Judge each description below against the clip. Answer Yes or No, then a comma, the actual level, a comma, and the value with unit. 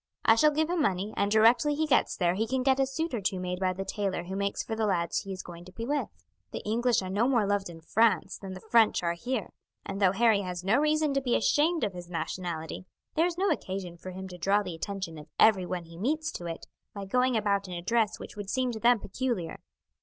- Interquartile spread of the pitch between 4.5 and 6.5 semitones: Yes, average, 5.2 semitones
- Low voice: No, high, 205 Hz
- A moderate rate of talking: No, fast, 255 wpm